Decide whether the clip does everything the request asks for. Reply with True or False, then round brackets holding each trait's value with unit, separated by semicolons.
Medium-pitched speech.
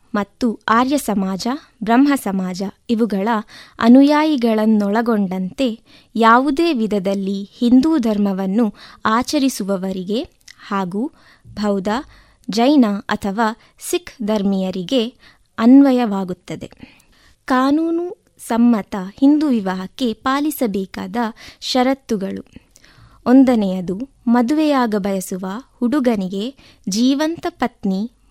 False (230 Hz)